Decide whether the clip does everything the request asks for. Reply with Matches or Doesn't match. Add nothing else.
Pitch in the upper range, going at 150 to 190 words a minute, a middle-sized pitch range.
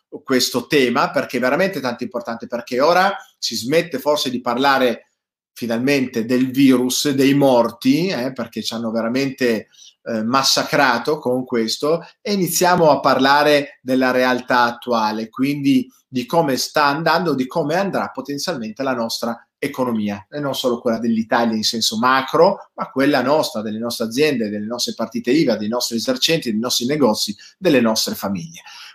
Doesn't match